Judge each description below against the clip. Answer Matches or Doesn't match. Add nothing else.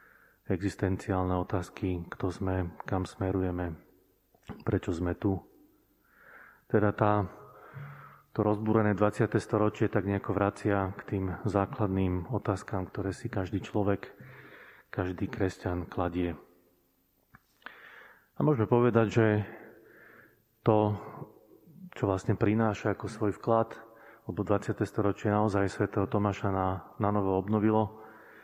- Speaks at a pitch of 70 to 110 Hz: Matches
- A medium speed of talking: Doesn't match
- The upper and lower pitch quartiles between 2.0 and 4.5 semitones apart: Matches